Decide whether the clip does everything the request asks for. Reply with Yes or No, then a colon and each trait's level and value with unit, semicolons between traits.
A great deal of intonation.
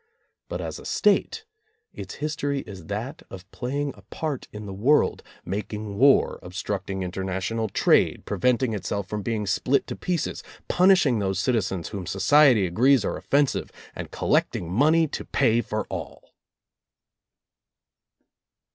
Yes: wide, 6.3 semitones